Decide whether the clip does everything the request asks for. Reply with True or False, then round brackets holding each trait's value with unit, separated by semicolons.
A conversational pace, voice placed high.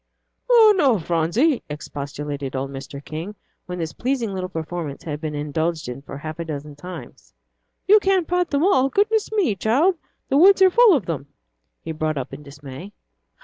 False (185 wpm; 170 Hz)